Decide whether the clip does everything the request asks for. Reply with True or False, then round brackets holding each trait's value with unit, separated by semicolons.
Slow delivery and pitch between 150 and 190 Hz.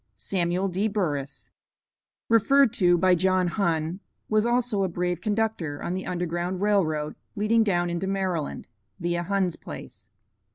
False (150 wpm; 185 Hz)